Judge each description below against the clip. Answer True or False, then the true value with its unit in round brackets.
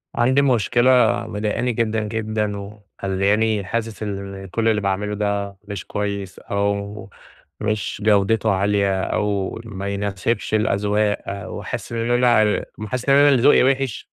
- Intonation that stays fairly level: True (2.2 semitones)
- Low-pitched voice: True (105 Hz)